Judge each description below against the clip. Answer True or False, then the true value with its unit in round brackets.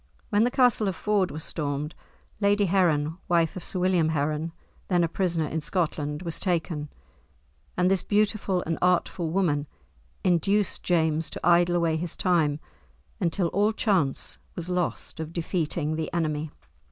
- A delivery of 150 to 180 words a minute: True (155 wpm)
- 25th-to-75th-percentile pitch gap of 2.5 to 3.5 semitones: True (2.9 semitones)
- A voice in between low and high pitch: True (170 Hz)